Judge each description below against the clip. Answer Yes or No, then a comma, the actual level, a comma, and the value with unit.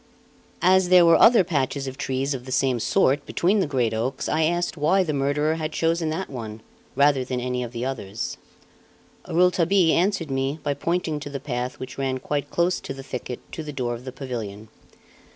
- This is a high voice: No, medium, 140 Hz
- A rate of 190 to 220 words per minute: Yes, average, 200 wpm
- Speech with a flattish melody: No, average, 4.4 semitones